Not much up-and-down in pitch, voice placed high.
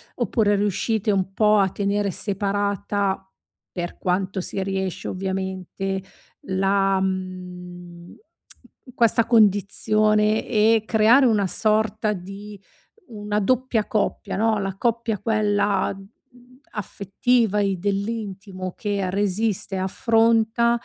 Yes: narrow, 2.3 semitones; high, 205 Hz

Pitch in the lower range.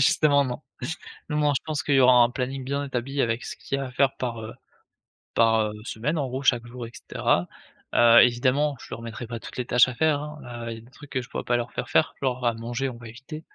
Yes: low, 125 Hz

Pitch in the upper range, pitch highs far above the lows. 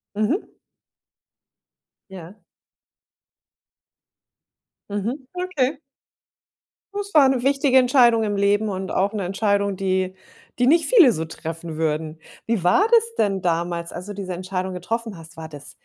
Yes: high, 200 Hz; wide, 6.0 semitones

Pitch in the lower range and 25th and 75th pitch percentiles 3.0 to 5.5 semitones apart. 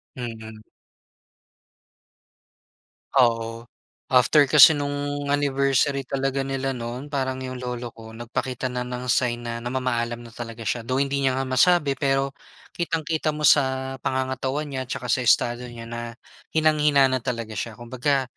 No: low, 130 Hz; narrow, 2.6 semitones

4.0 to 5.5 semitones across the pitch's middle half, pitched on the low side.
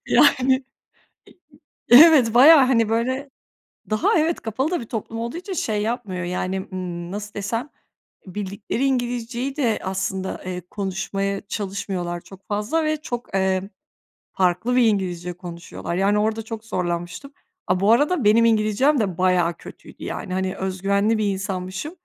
No: average, 4.5 semitones; high, 210 Hz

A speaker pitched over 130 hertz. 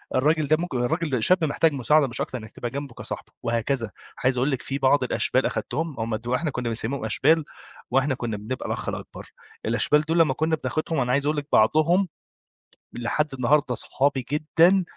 Yes: medium, 140 Hz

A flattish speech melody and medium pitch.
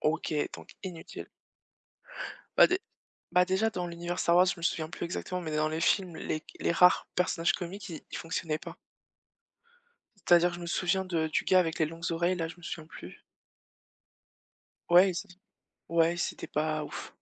Yes: narrow, 1.8 semitones; medium, 170 Hz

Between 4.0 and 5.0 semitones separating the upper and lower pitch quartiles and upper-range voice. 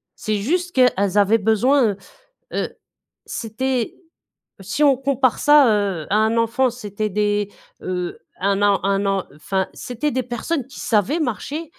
Yes: average, 4.6 semitones; high, 220 Hz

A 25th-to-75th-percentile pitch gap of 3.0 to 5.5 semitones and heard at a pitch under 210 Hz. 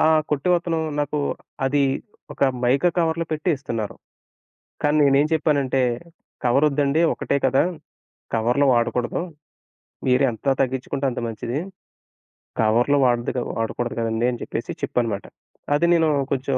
Yes: average, 3.4 semitones; low, 135 Hz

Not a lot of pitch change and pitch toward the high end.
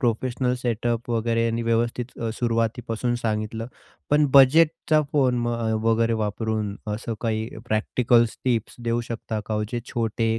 No: narrow, 1.5 semitones; low, 115 Hz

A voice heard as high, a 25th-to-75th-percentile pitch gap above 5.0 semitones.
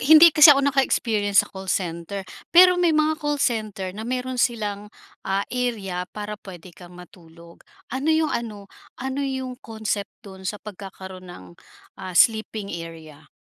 Yes: high, 210 Hz; wide, 5.6 semitones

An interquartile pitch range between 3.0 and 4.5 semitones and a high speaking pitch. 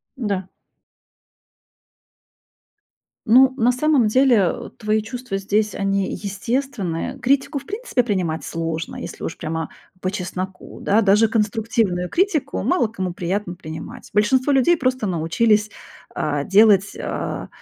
No: average, 5.1 semitones; high, 210 Hz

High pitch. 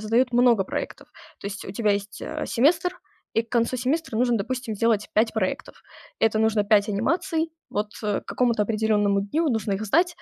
Yes: high, 225 Hz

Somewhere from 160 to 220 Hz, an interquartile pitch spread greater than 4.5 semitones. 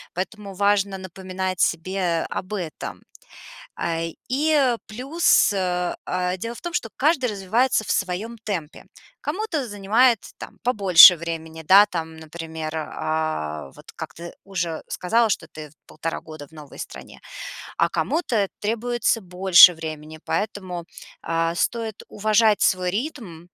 Yes: medium, 185 Hz; average, 5.0 semitones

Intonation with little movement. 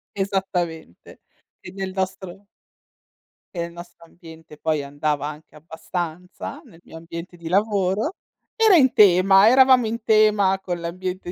No: average, 3.2 semitones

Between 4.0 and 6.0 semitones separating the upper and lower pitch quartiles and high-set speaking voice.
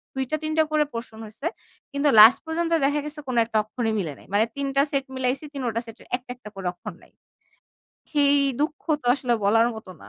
Yes: average, 4.6 semitones; very high, 255 Hz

